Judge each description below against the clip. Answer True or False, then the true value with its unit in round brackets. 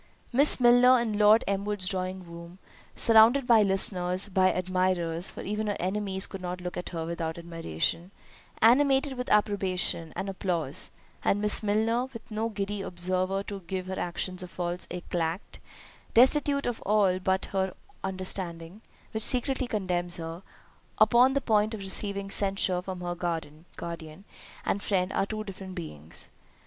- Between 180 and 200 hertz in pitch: True (190 Hz)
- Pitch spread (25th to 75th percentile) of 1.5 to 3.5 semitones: True (3.1 semitones)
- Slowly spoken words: False (150 wpm)